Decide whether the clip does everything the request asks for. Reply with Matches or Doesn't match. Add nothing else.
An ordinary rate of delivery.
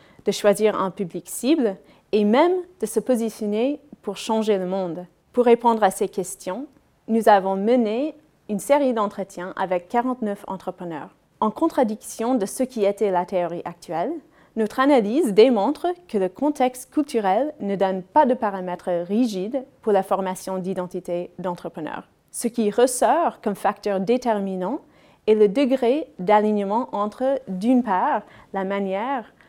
Doesn't match